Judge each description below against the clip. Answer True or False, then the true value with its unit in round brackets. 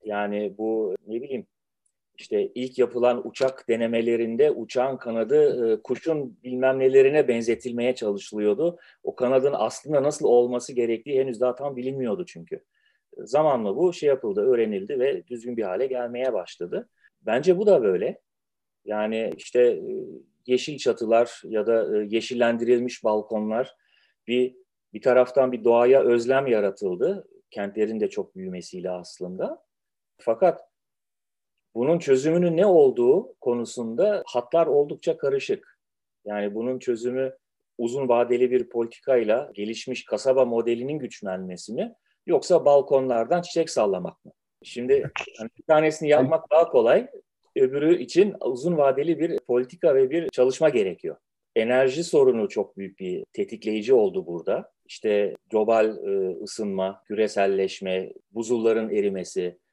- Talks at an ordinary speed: True (120 wpm)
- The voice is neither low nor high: False (130 Hz)